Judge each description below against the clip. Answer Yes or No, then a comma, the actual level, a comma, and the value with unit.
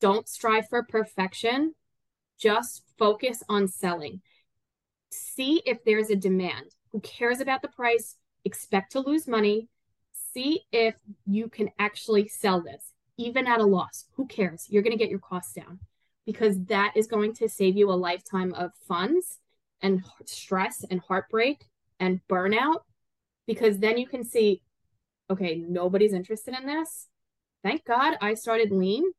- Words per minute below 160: Yes, average, 150 wpm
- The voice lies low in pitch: No, high, 215 Hz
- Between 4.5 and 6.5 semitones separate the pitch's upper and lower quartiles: No, average, 3.6 semitones